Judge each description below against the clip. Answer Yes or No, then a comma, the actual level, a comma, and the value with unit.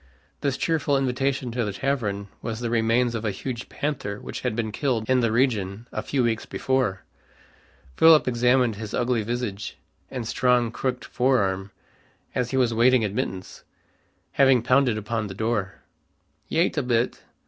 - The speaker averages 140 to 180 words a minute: Yes, average, 160 wpm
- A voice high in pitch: No, low, 120 Hz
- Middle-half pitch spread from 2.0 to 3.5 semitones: Yes, average, 3.0 semitones